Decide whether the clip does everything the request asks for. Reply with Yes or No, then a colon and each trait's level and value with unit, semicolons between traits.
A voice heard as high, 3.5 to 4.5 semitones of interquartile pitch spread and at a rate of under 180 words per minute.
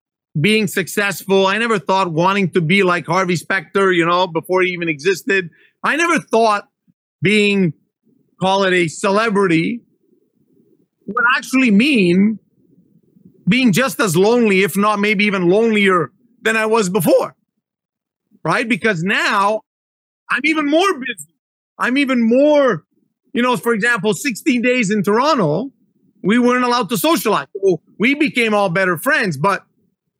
Yes: high, 210 Hz; average, 4.0 semitones; average, 140 wpm